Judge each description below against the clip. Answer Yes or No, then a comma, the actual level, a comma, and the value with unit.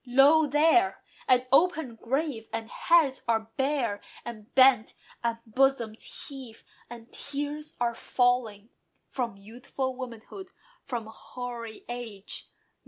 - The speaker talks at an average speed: No, slow, 110 wpm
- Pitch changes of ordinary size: Yes, average, 3.4 semitones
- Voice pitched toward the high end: Yes, high, 245 Hz